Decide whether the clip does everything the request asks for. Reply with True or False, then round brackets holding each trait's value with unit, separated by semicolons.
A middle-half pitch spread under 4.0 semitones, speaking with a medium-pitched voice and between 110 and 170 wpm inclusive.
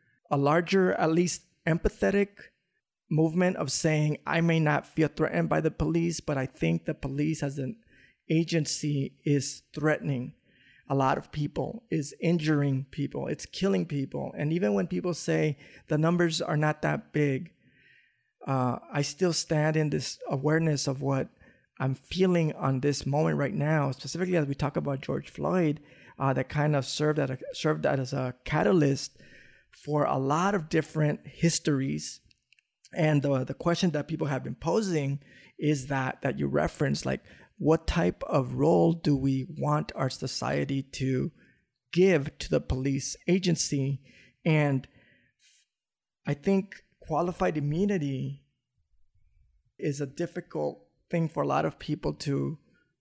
True (3.4 semitones; 150 Hz; 150 wpm)